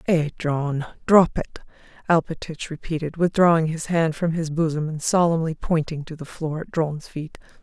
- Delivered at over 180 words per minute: No, average, 165 wpm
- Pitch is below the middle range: No, medium, 160 Hz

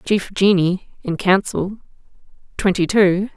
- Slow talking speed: Yes, slow, 105 wpm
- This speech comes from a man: No, female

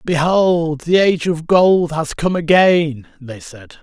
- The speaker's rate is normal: Yes, average, 155 wpm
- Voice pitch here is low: No, medium, 165 Hz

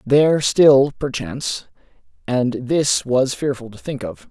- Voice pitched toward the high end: No, low, 125 Hz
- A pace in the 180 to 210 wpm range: No, average, 140 wpm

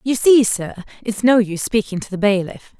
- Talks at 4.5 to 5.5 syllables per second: Yes, 5.2 syllables/s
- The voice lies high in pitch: Yes, high, 215 Hz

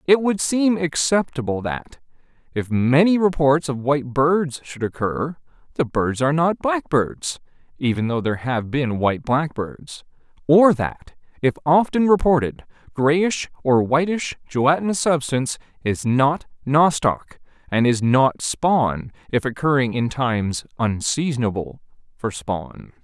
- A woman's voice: No, male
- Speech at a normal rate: No, slow, 130 wpm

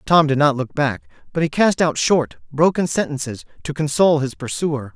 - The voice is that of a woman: No, male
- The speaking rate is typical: Yes, average, 195 wpm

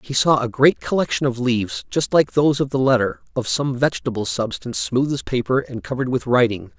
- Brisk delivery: Yes, fast, 210 wpm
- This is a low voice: Yes, low, 130 Hz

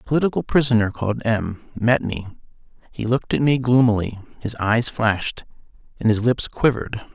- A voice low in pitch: Yes, low, 115 Hz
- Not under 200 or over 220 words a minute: No, average, 160 wpm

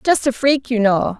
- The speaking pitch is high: Yes, high, 245 Hz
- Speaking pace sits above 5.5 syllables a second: No, 4.6 syllables/s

